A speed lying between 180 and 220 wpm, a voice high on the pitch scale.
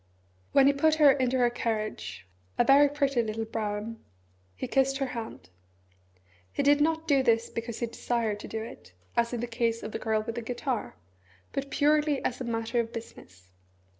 Yes: average, 190 wpm; high, 235 Hz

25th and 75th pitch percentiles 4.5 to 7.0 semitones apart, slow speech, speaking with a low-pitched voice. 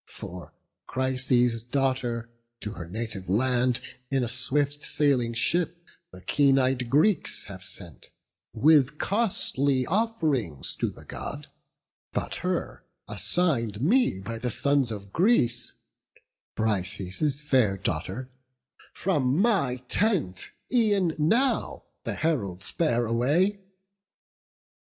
Yes: wide, 5.6 semitones; slow, 110 wpm; low, 130 Hz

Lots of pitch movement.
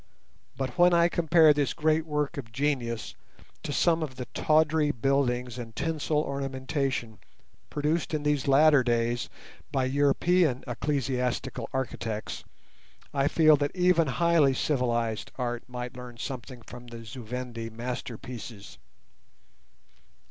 No: average, 3.6 semitones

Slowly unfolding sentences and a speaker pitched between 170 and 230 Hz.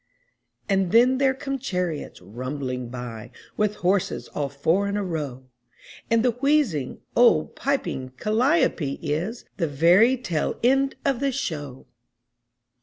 Yes: slow, 130 wpm; high, 190 Hz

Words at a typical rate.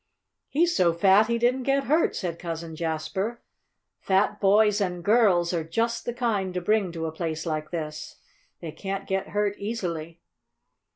Yes: average, 165 wpm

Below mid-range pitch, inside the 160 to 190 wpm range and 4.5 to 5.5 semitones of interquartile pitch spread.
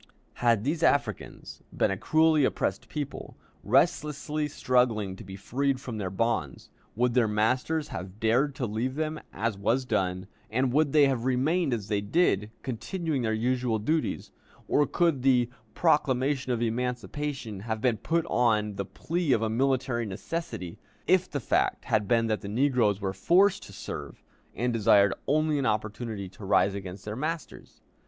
Yes: low, 120 Hz; average, 165 wpm; average, 5.2 semitones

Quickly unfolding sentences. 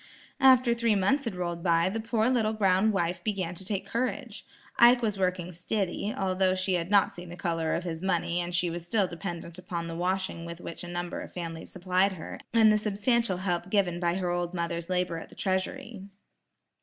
Yes: fast, 210 wpm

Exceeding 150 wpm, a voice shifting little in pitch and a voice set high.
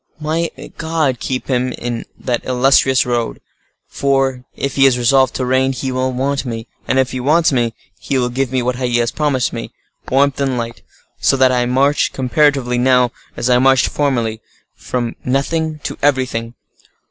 No: average, 170 wpm; narrow, 1.9 semitones; low, 130 Hz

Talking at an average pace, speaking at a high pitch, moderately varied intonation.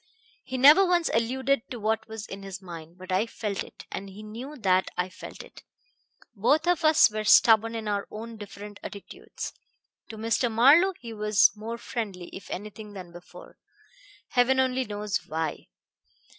Yes: average, 165 wpm; high, 215 Hz; average, 3.9 semitones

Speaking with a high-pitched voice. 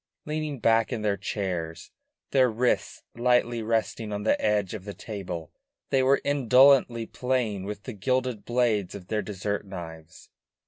No: low, 110 Hz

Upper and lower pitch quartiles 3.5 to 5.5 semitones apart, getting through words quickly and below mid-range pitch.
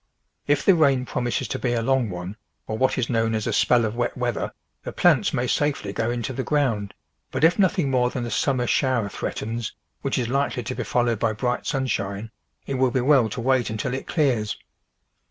No: average, 2.8 semitones; fast, 210 wpm; low, 125 Hz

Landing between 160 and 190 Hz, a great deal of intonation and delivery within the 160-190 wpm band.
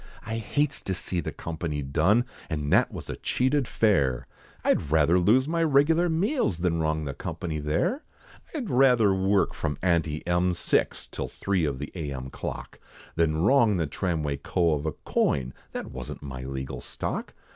No: very low, 85 Hz; wide, 7.3 semitones; average, 170 wpm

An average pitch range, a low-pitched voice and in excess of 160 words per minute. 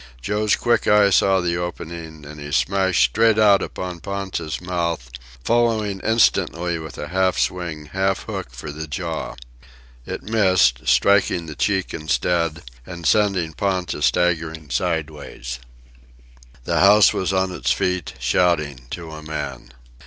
No: average, 3.8 semitones; very low, 85 Hz; average, 140 wpm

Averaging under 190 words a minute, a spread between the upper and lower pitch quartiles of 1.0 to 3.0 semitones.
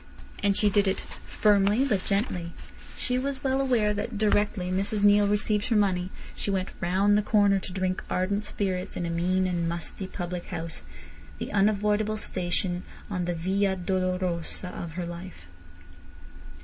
Yes: average, 155 wpm; narrow, 2.6 semitones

